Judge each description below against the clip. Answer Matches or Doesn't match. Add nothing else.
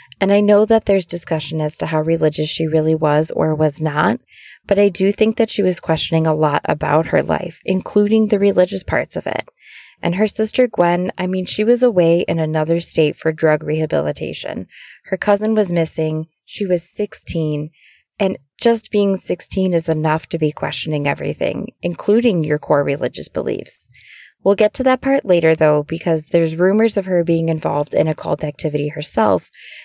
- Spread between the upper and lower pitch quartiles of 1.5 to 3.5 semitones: Doesn't match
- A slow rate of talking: Doesn't match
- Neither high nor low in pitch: Matches